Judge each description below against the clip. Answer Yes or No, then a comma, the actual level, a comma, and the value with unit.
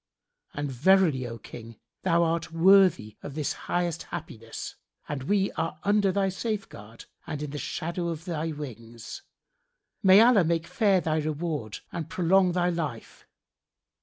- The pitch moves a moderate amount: Yes, average, 4.5 semitones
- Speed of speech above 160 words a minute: No, average, 145 wpm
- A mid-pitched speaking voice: Yes, medium, 165 Hz